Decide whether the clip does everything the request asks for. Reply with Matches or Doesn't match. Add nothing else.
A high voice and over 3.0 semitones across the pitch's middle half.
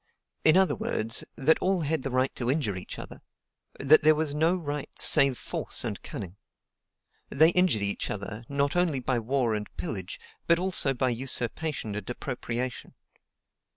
Doesn't match